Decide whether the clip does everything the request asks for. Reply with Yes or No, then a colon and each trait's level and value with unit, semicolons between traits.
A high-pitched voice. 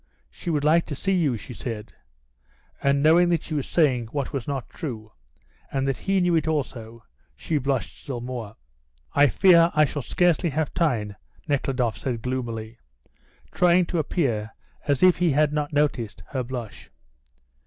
No: medium, 140 Hz